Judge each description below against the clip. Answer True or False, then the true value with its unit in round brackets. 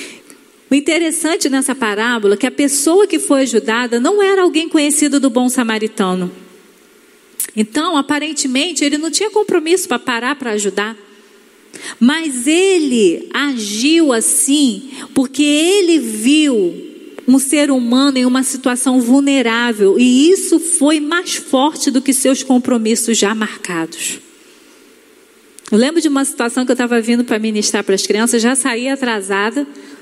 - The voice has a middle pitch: False (270 Hz)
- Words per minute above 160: False (140 wpm)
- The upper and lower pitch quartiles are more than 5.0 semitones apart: True (5.6 semitones)